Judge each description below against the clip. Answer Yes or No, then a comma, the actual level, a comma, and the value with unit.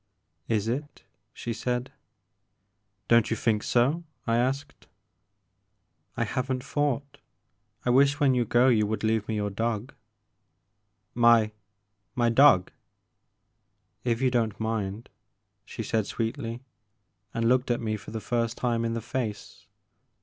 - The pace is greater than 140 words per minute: No, slow, 135 wpm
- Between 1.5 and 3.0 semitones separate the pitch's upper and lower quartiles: Yes, narrow, 2.4 semitones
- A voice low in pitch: Yes, low, 115 Hz